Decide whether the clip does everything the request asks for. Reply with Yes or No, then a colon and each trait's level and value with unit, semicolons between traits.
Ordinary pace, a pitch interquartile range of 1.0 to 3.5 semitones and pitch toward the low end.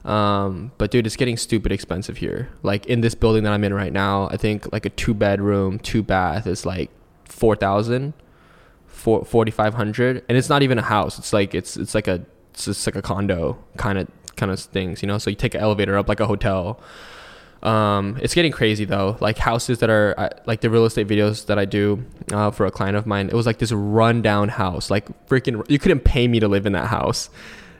No: fast, 225 wpm; narrow, 2.5 semitones; low, 105 Hz